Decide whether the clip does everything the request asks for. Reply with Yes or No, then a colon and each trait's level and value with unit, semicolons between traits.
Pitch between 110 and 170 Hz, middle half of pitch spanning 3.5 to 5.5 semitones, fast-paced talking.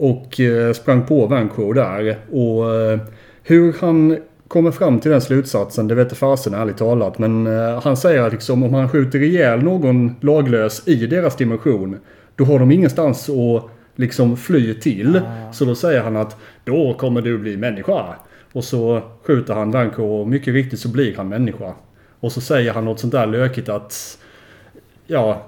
No: low, 120 Hz; average, 3.8 semitones; average, 170 wpm